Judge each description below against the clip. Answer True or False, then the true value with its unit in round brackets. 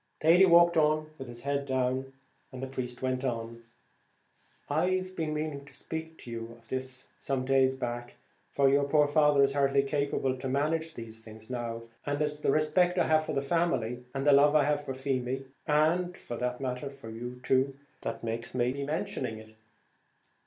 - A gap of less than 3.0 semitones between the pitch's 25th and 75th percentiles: False (3.4 semitones)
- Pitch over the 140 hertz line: False (135 Hz)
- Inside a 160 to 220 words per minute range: True (195 wpm)